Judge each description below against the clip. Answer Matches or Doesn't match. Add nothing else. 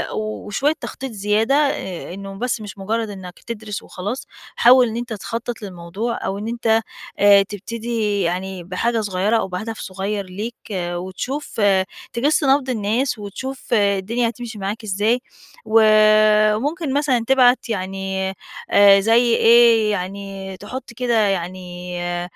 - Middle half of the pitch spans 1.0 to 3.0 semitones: Doesn't match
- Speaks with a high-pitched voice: Matches